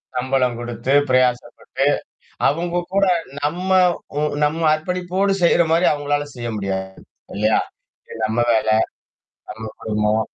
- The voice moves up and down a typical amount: No, wide, 7.0 semitones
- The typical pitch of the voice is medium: No, low, 130 Hz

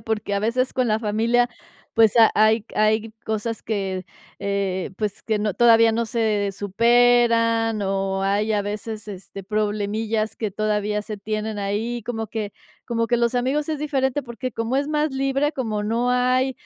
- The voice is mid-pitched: No, high, 220 Hz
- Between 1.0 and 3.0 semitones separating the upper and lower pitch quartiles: Yes, narrow, 2.5 semitones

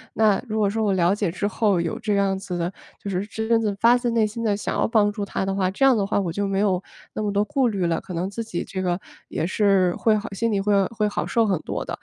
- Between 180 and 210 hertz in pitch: Yes, high, 200 Hz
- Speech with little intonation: Yes, narrow, 2.3 semitones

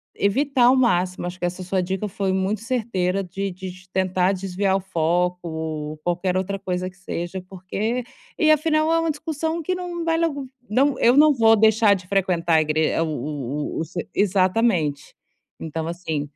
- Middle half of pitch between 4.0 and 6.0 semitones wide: Yes, average, 5.1 semitones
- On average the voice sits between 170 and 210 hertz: Yes, high, 190 Hz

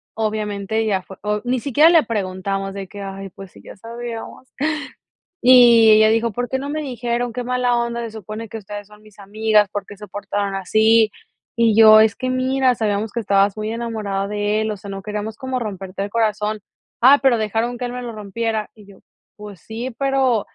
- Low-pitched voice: No, high, 220 Hz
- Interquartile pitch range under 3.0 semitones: Yes, narrow, 2.6 semitones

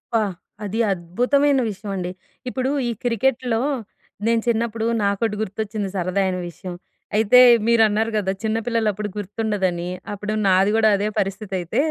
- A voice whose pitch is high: Yes, high, 210 Hz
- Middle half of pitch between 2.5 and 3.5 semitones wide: Yes, average, 2.8 semitones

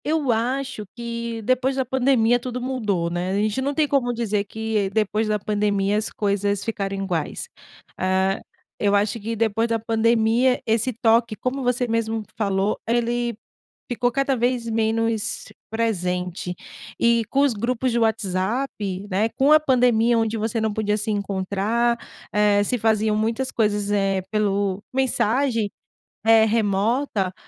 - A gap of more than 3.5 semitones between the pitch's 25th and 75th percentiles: No, average, 2.8 semitones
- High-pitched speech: Yes, high, 225 Hz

